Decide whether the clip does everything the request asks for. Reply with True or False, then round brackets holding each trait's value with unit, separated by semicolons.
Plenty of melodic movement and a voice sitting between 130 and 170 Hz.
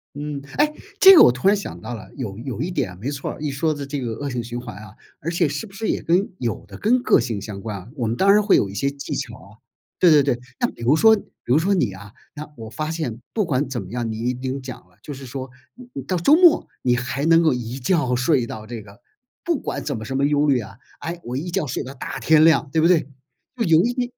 True (5.7 semitones; 140 Hz)